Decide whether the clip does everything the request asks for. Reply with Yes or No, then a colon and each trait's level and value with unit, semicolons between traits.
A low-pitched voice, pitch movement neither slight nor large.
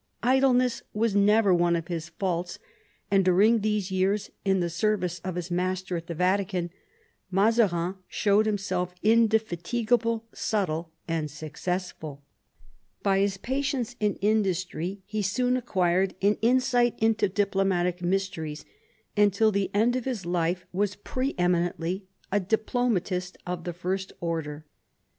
No: high, 190 Hz; average, 3.5 semitones